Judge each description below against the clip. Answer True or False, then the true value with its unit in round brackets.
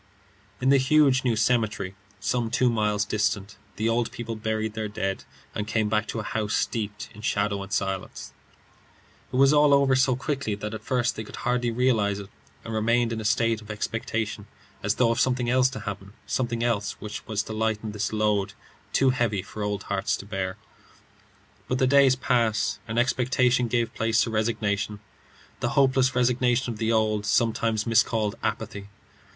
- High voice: False (110 Hz)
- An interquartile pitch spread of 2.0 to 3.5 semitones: True (2.8 semitones)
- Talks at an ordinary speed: True (180 wpm)